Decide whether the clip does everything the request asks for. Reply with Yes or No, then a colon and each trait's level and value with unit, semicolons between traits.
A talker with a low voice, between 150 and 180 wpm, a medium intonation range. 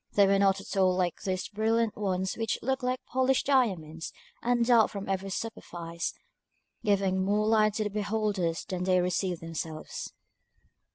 No: high, 200 Hz; average, 160 wpm; average, 3.3 semitones